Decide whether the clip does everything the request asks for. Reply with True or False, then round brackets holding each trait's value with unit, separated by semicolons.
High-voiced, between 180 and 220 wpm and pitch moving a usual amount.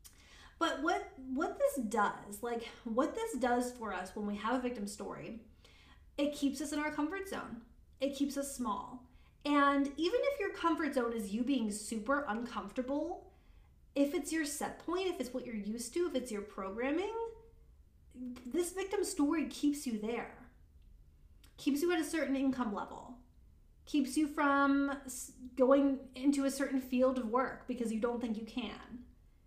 False (265 Hz; 170 wpm; 3.9 semitones)